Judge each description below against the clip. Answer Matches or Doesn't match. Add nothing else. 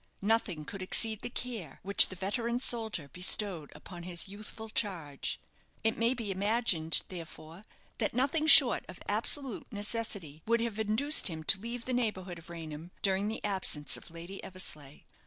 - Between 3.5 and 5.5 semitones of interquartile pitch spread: Matches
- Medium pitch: Doesn't match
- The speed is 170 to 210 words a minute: Doesn't match